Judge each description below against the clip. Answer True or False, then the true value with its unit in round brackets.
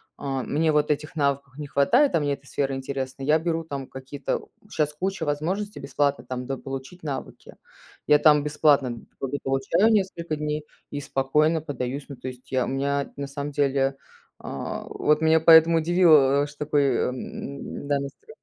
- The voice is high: False (145 Hz)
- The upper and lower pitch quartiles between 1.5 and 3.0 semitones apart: True (2.4 semitones)